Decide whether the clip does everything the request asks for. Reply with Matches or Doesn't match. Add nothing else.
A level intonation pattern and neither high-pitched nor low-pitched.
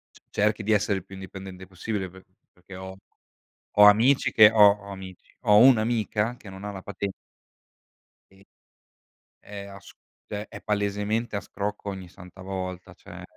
Doesn't match